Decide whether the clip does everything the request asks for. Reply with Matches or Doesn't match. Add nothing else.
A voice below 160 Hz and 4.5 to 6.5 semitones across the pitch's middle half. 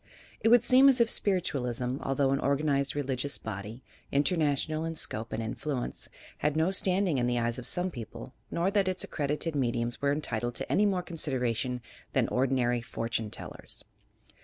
Matches